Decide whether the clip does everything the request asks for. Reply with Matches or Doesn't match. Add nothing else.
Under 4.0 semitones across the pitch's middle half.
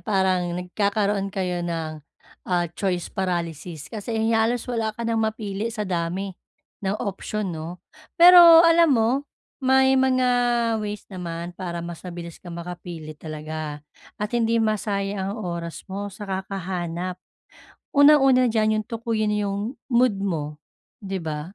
Doesn't match